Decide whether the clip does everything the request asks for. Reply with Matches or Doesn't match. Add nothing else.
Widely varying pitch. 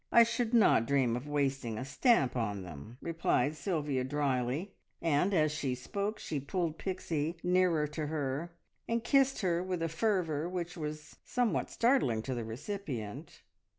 Matches